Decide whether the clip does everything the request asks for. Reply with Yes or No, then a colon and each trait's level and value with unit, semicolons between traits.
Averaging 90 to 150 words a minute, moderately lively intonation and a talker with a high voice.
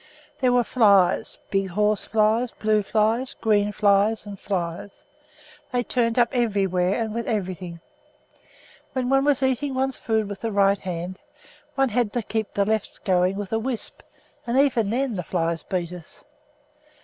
No: average, 160 wpm; average, 3.6 semitones; high, 215 Hz